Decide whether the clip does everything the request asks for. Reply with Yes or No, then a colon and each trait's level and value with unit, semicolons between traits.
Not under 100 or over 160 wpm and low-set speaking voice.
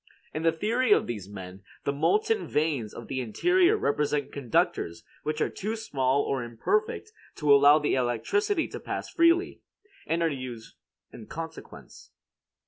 No: average, 150 wpm; medium, 150 Hz